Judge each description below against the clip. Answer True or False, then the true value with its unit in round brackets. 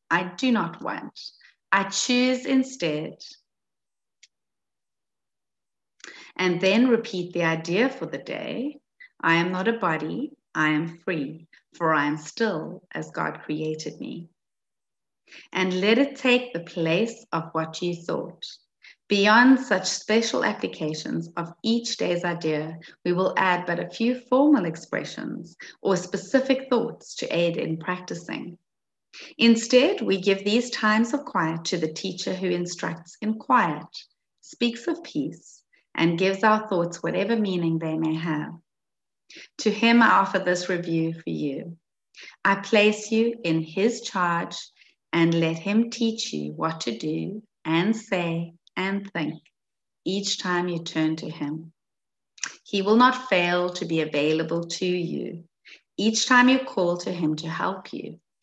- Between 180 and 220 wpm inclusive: False (145 wpm)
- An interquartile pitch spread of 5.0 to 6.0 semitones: True (5.5 semitones)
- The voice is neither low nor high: True (180 Hz)